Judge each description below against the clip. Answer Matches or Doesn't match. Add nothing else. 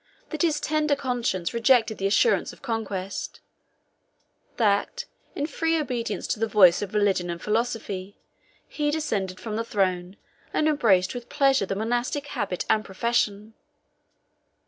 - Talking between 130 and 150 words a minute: Matches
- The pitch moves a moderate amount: Doesn't match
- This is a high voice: Matches